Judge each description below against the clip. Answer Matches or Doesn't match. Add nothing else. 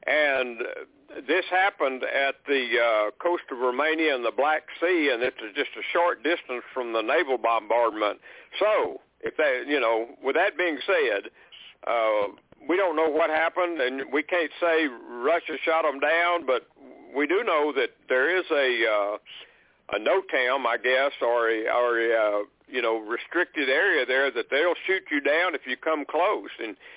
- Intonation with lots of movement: Matches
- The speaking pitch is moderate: Matches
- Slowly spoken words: Doesn't match